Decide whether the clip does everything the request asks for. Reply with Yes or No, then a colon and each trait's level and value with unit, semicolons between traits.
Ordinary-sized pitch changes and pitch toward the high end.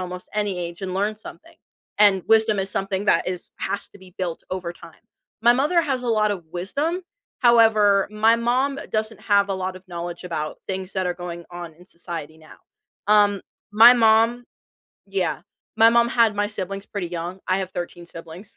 Yes: average, 3.7 semitones; high, 195 Hz